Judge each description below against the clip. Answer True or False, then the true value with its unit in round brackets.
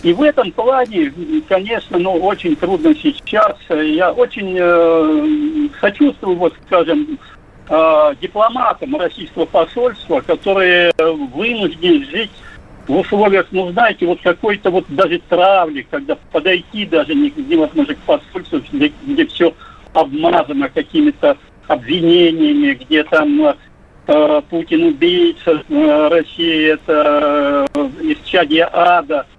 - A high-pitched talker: True (235 Hz)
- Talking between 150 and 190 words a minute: False (110 wpm)